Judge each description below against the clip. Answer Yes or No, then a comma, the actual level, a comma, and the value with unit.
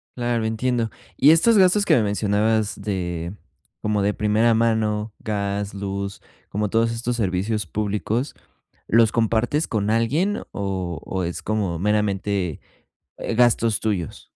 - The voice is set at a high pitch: No, low, 105 Hz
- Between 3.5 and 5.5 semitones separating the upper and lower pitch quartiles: No, narrow, 2.4 semitones